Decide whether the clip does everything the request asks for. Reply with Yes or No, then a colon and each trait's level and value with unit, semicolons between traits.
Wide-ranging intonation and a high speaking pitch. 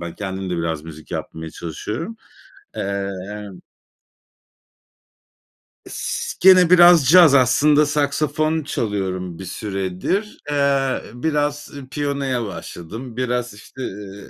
No: wide, 7.3 semitones; low, 120 Hz